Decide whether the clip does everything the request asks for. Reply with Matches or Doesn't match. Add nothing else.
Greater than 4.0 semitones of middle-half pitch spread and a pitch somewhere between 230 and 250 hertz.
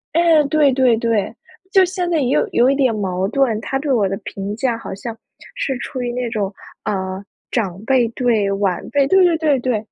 Matches